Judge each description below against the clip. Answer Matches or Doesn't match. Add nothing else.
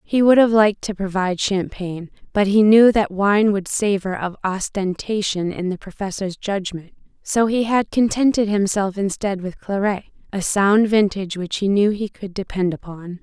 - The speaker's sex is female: Matches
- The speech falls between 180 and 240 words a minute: Doesn't match